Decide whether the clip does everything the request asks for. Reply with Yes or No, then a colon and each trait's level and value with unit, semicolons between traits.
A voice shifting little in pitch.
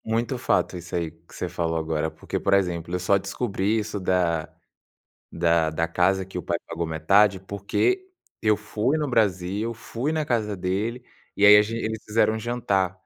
No: average, 4.2 semitones